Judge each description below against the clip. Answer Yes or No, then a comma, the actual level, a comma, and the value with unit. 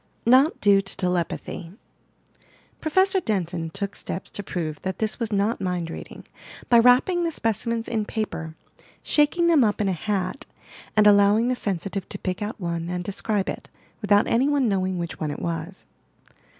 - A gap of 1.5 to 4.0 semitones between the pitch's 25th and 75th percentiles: No, average, 4.4 semitones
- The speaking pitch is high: Yes, high, 205 Hz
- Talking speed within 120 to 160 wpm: No, average, 170 wpm